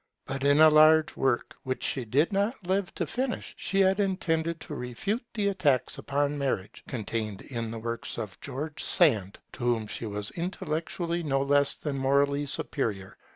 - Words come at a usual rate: Yes, average, 170 wpm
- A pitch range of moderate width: No, wide, 6.0 semitones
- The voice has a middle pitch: Yes, medium, 145 Hz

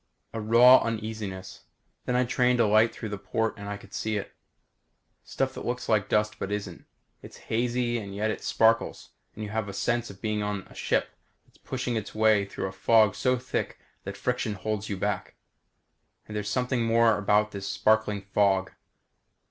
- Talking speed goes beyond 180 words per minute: Yes, average, 190 wpm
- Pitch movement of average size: No, narrow, 2.3 semitones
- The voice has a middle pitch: No, low, 110 Hz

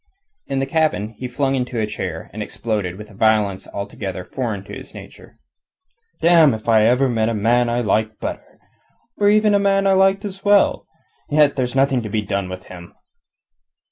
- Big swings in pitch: Yes, wide, 5.7 semitones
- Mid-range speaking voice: No, low, 120 Hz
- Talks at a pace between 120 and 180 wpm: No, average, 190 wpm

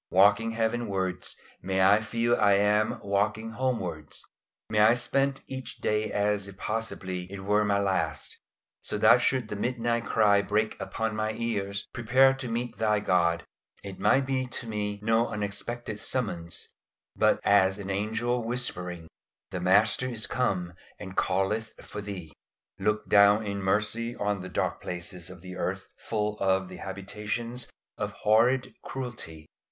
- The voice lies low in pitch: Yes, low, 105 Hz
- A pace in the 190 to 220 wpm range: No, average, 150 wpm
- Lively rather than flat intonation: No, average, 3.2 semitones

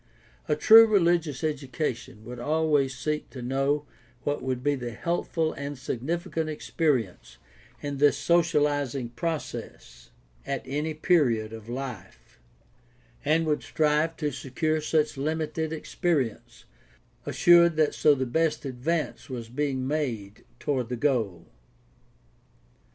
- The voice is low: No, medium, 145 Hz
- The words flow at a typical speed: No, slow, 125 wpm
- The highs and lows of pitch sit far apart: No, average, 3.7 semitones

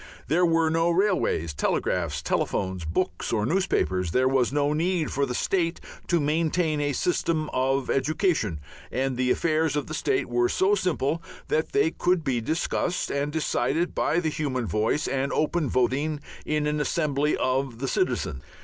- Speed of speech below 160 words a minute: No, average, 165 wpm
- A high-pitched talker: No, medium, 150 Hz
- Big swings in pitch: No, average, 4.2 semitones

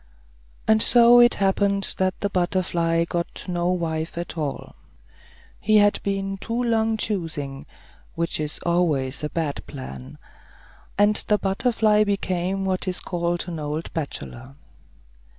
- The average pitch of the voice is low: No, medium, 180 Hz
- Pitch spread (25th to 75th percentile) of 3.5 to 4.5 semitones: Yes, average, 3.9 semitones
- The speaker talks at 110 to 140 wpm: Yes, slow, 135 wpm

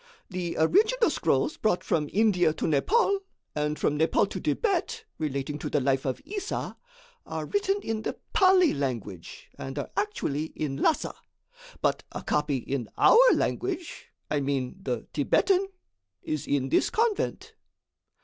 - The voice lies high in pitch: No, medium, 160 Hz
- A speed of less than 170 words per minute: Yes, average, 145 wpm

